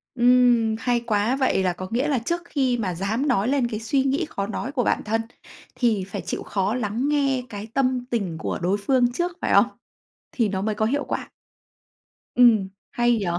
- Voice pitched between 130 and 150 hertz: No, high, 240 Hz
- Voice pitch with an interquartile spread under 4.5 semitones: Yes, average, 4.0 semitones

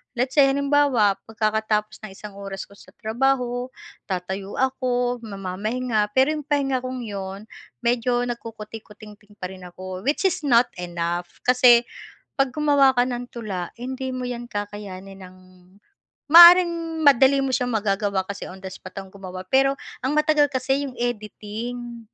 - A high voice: Yes, high, 235 Hz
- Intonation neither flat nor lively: Yes, average, 4.7 semitones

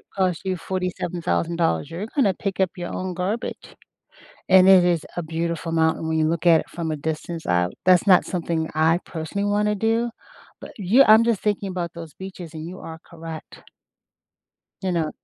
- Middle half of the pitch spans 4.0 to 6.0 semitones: No, average, 2.8 semitones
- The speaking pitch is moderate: Yes, medium, 175 Hz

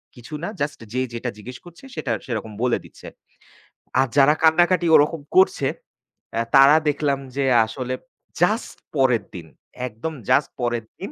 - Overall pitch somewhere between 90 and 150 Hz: Yes, low, 135 Hz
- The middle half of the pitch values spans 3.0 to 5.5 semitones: Yes, average, 4.6 semitones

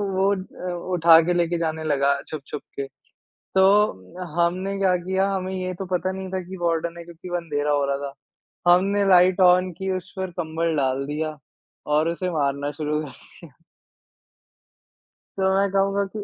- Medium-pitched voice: Yes, medium, 175 Hz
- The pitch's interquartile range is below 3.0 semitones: No, average, 3.3 semitones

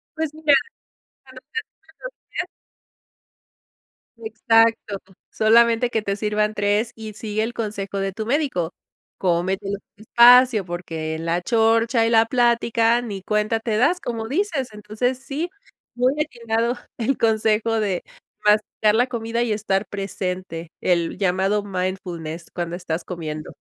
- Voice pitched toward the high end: Yes, high, 220 Hz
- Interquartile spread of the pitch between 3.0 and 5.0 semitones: Yes, average, 3.5 semitones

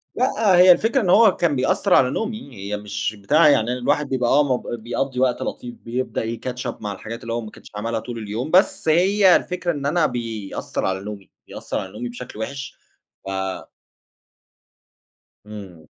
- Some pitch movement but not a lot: No, wide, 7.0 semitones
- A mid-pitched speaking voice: No, low, 125 Hz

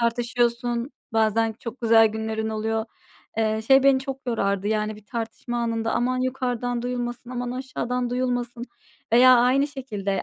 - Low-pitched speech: No, high, 240 Hz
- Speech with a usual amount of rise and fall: No, narrow, 2.1 semitones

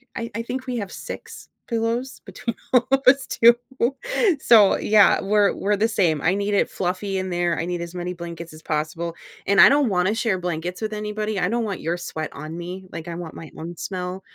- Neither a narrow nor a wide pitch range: Yes, average, 4.0 semitones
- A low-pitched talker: No, high, 190 Hz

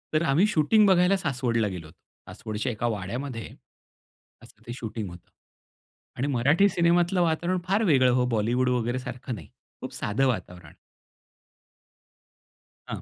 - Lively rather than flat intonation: Yes, wide, 7.0 semitones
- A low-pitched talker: Yes, low, 125 Hz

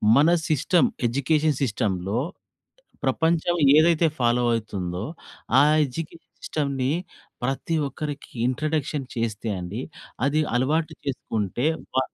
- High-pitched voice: No, low, 135 Hz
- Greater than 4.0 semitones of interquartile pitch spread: Yes, average, 5.0 semitones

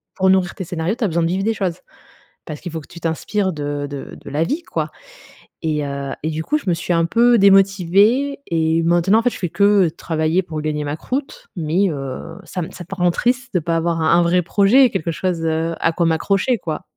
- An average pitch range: Yes, average, 3.7 semitones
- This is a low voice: No, medium, 175 Hz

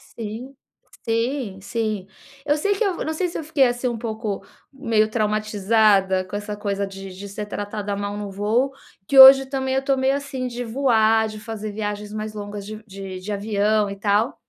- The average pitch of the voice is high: Yes, high, 215 Hz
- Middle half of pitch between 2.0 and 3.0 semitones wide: No, average, 3.7 semitones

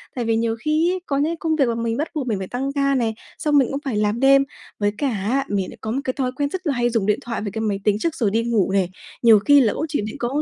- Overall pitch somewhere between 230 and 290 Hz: Yes, high, 240 Hz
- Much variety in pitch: No, average, 4.5 semitones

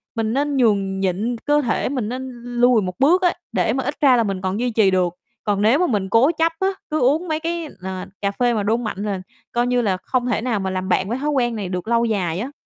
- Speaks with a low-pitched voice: No, high, 230 Hz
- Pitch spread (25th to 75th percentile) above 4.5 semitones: Yes, average, 5.1 semitones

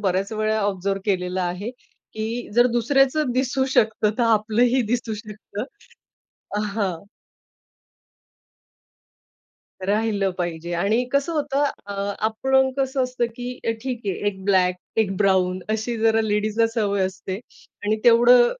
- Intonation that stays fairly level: No, average, 3.6 semitones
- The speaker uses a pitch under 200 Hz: No, high, 220 Hz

